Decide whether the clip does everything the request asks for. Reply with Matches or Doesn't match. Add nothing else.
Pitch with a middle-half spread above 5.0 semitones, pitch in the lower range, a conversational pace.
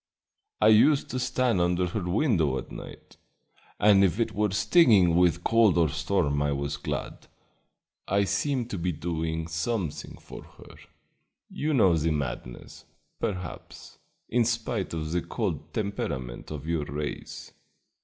Matches